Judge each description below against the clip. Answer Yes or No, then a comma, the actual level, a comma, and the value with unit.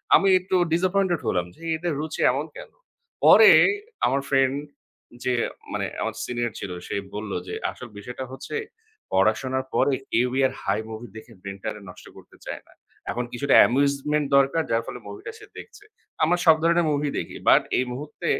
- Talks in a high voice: No, low, 135 Hz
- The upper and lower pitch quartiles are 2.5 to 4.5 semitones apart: No, average, 4.9 semitones